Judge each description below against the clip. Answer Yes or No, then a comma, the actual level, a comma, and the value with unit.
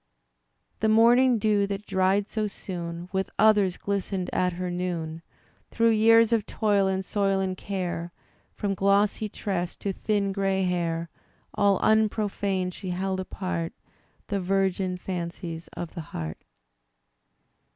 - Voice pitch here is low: No, high, 195 Hz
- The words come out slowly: Yes, slow, 130 wpm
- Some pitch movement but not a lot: No, narrow, 2.3 semitones